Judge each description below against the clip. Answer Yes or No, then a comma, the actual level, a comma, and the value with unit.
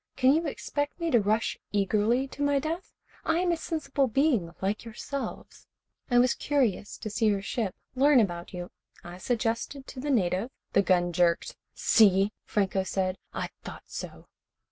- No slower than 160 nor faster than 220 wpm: Yes, average, 170 wpm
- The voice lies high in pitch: Yes, high, 225 Hz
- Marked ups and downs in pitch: Yes, wide, 6.4 semitones